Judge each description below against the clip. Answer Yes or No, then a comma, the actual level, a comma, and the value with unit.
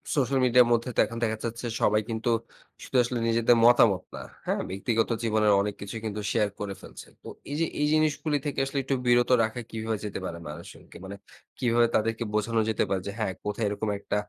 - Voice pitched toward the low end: Yes, low, 115 Hz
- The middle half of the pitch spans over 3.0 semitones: No, narrow, 2.6 semitones